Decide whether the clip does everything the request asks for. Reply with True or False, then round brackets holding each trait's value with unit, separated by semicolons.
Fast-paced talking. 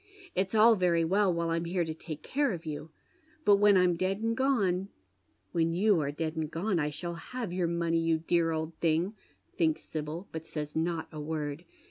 True (210 wpm)